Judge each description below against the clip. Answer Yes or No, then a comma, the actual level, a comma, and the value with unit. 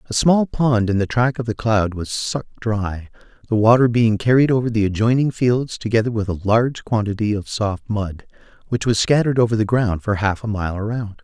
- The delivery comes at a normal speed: No, fast, 210 wpm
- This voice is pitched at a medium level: No, low, 110 Hz